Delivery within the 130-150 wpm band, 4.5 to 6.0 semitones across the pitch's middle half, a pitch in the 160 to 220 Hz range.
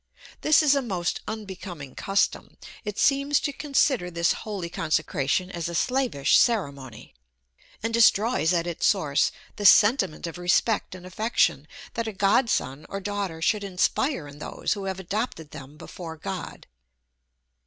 Yes: average, 145 wpm; average, 5.3 semitones; high, 190 Hz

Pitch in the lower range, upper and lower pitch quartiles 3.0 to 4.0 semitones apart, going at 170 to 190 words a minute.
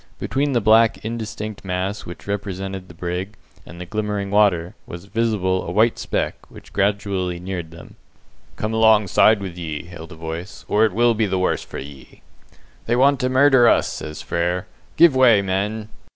Yes: low, 100 Hz; average, 3.7 semitones; average, 175 wpm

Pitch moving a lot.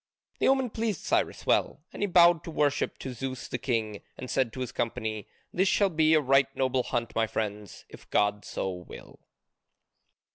Yes: wide, 6.9 semitones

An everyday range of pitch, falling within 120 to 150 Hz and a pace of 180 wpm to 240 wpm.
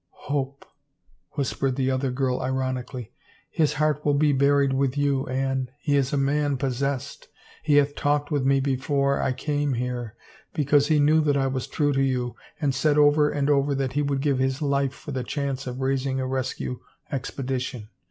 No: narrow, 1.7 semitones; medium, 140 Hz; average, 195 wpm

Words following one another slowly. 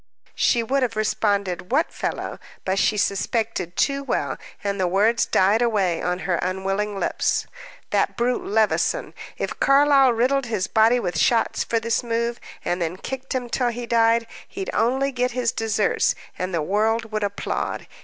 No: average, 165 wpm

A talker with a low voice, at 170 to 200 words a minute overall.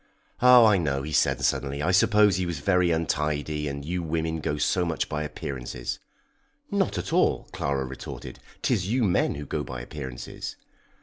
Yes: very low, 75 Hz; average, 175 wpm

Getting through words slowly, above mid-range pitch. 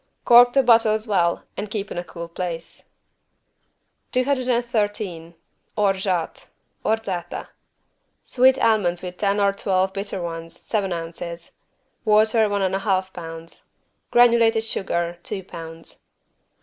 Yes: slow, 115 wpm; high, 195 Hz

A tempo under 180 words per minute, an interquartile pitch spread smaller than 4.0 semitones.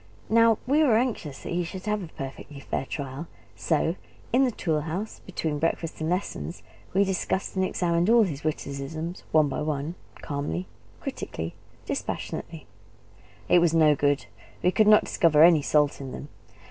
No: average, 165 wpm; average, 4.4 semitones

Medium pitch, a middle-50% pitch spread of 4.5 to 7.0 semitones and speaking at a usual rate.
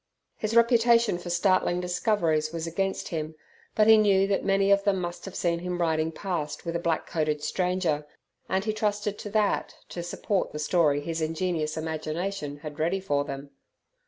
No: medium, 175 Hz; average, 3.9 semitones; average, 180 wpm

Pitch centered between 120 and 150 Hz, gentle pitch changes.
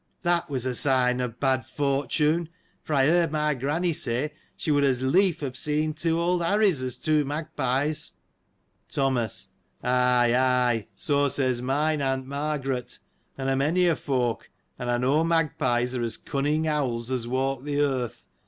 No: medium, 140 Hz; average, 3.3 semitones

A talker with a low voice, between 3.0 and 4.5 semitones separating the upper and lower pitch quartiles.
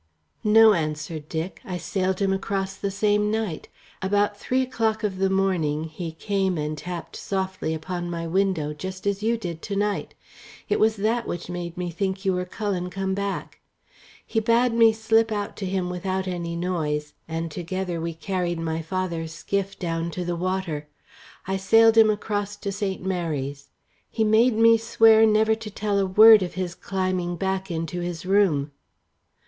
No: high, 190 Hz; average, 3.3 semitones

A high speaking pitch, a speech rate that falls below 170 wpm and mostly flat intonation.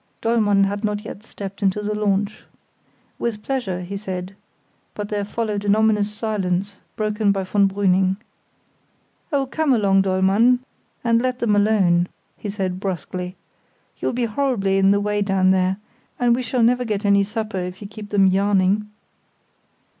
Yes: high, 205 Hz; average, 160 wpm; narrow, 2.1 semitones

